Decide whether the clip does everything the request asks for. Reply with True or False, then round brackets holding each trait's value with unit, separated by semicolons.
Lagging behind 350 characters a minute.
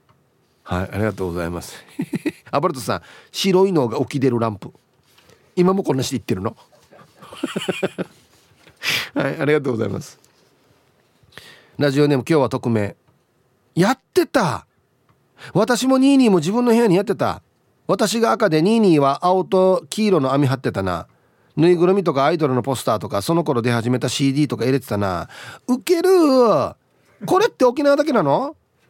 True (315 characters per minute)